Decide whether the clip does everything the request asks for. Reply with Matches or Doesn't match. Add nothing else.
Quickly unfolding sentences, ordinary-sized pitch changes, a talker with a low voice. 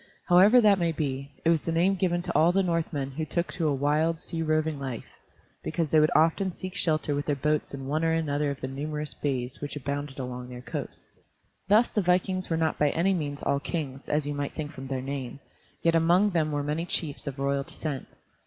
Doesn't match